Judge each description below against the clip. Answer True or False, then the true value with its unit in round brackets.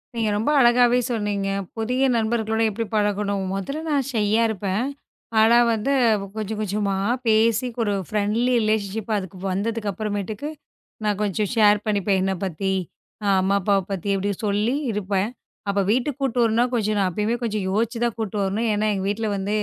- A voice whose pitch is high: True (215 Hz)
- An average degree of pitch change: False (2.2 semitones)